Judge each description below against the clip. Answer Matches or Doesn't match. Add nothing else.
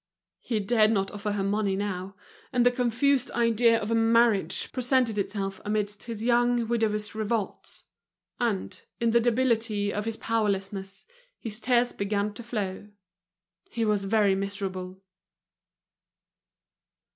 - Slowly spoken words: Matches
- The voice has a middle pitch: Doesn't match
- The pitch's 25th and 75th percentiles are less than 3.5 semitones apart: Matches